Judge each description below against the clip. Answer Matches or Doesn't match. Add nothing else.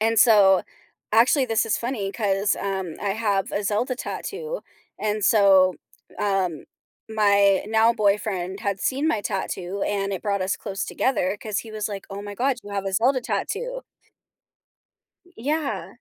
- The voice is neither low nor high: Doesn't match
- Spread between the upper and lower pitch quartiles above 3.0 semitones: Doesn't match